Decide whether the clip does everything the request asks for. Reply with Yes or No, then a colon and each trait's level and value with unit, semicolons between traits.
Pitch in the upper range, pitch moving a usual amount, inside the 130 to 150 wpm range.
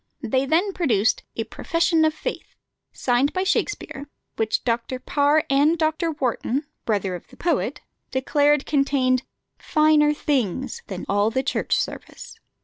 Yes: very high, 275 Hz; average, 4.2 semitones; average, 140 wpm